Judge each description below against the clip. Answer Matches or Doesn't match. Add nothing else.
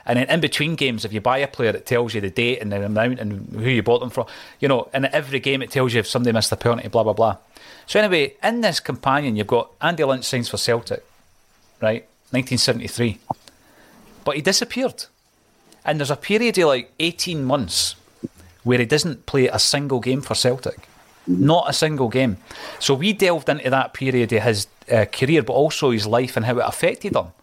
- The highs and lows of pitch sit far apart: Doesn't match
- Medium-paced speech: Doesn't match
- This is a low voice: Matches